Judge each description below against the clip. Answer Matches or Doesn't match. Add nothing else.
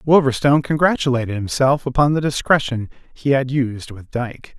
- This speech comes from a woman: Doesn't match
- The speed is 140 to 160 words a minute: Matches